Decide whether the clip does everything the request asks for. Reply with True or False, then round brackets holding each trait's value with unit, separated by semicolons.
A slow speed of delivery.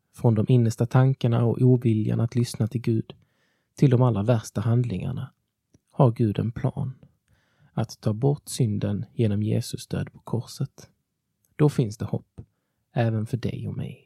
False (160 wpm)